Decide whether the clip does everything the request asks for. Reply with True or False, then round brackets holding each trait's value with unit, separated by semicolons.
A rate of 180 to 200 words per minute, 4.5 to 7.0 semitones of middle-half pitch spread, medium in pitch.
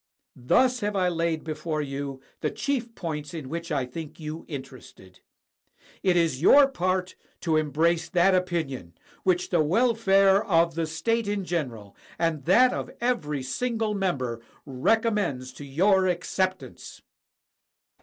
False (135 wpm; 4.9 semitones; 170 Hz)